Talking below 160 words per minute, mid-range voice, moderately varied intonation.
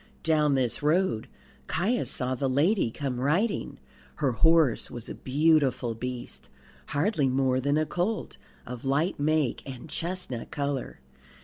Yes: slow, 135 wpm; medium, 145 Hz; average, 4.1 semitones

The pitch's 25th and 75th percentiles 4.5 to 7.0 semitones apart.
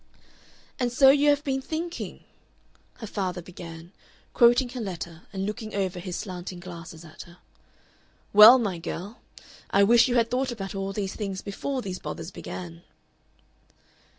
Yes: wide, 5.4 semitones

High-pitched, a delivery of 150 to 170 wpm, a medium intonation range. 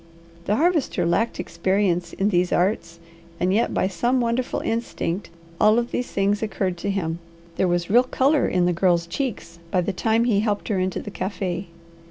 No: high, 195 Hz; average, 185 wpm; average, 4.4 semitones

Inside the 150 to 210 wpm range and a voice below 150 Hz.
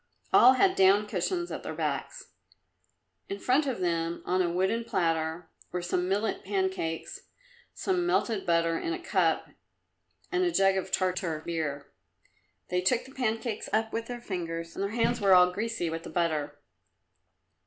No: average, 165 wpm; high, 190 Hz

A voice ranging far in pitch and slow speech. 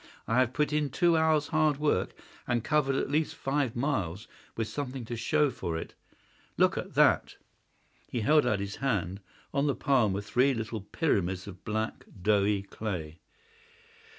No: wide, 6.2 semitones; average, 165 wpm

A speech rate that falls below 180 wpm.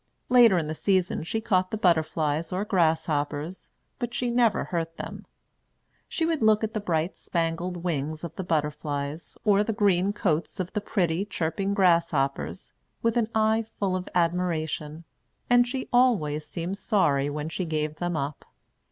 Yes: average, 160 wpm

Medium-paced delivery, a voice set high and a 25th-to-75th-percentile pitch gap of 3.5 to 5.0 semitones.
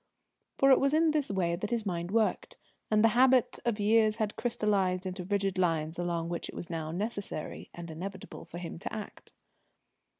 Yes: average, 190 wpm; high, 195 Hz; average, 4.5 semitones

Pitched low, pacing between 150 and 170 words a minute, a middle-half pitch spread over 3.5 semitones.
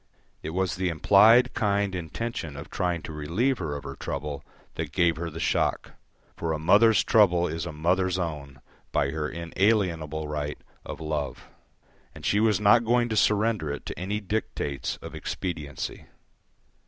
Yes: very low, 85 Hz; average, 165 wpm; average, 5.1 semitones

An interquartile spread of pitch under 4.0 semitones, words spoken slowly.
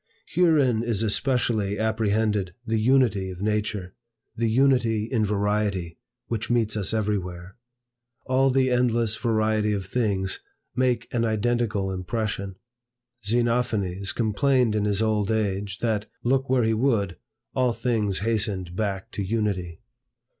Yes: average, 3.0 semitones; slow, 125 wpm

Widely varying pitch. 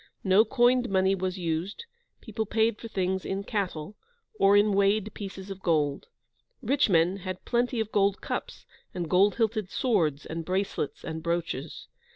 No: average, 3.5 semitones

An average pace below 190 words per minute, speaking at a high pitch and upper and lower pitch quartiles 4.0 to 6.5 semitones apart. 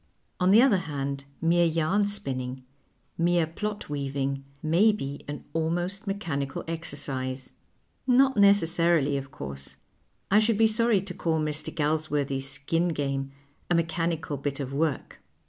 No: slow, 135 wpm; medium, 160 Hz; average, 4.8 semitones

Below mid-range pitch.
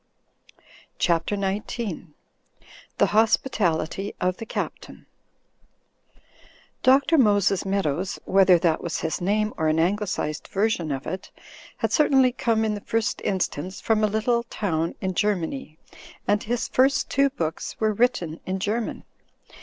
No: high, 200 Hz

